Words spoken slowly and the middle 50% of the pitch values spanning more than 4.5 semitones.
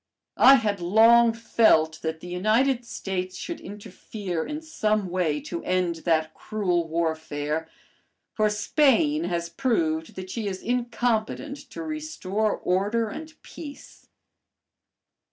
Yes: slow, 120 wpm; wide, 5.6 semitones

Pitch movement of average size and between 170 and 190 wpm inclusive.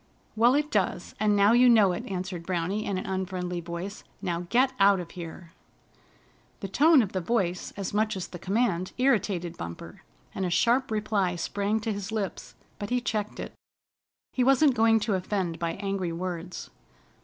Yes: average, 3.6 semitones; average, 180 wpm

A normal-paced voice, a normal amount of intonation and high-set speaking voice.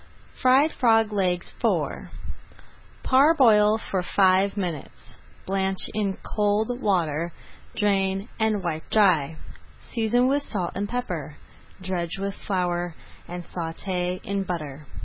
No: slow, 120 wpm; average, 3.5 semitones; high, 195 Hz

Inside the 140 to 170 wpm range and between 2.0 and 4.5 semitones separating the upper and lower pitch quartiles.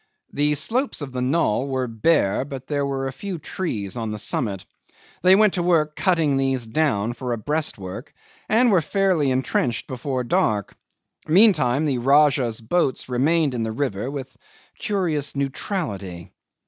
No: average, 155 wpm; average, 5.1 semitones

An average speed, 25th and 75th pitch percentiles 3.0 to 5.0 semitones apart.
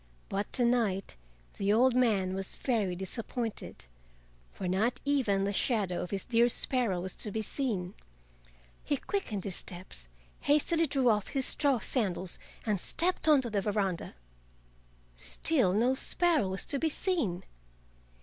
No: average, 150 wpm; wide, 5.4 semitones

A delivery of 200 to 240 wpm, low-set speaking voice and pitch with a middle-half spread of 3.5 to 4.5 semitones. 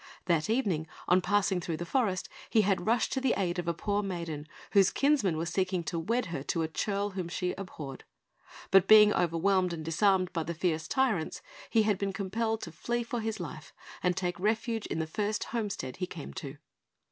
No: fast, 205 wpm; high, 190 Hz; average, 4.0 semitones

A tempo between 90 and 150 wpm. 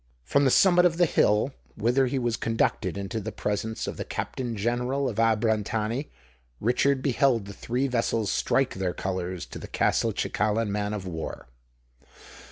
No: average, 160 wpm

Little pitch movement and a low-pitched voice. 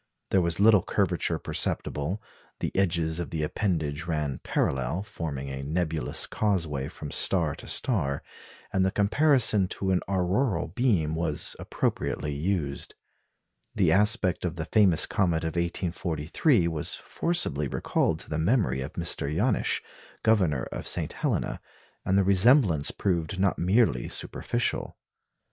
No: average, 4.6 semitones; very low, 85 Hz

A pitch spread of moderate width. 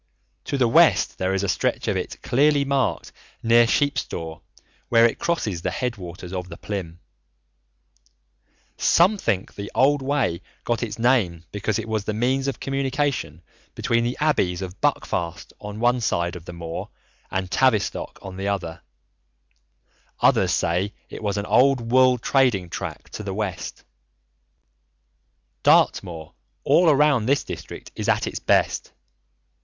No: wide, 6.2 semitones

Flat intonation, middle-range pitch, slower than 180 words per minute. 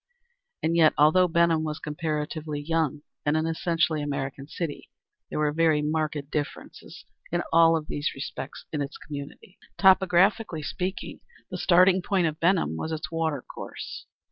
Yes: narrow, 2.3 semitones; medium, 155 Hz; average, 150 wpm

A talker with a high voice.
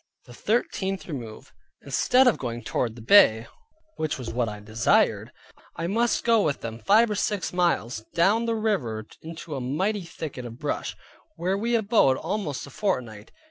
No: medium, 160 Hz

